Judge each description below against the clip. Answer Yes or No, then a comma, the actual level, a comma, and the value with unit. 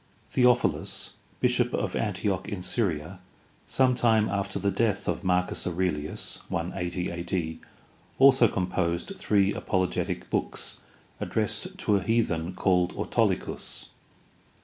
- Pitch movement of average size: Yes, average, 3.1 semitones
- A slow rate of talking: Yes, slow, 110 wpm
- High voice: No, very low, 95 Hz